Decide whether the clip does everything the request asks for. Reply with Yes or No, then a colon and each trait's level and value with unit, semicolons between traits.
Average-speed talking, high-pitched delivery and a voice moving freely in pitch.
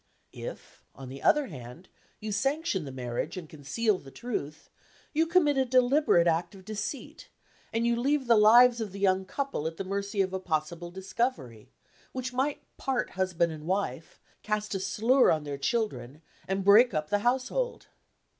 Yes: average, 175 wpm; high, 200 Hz; wide, 7.2 semitones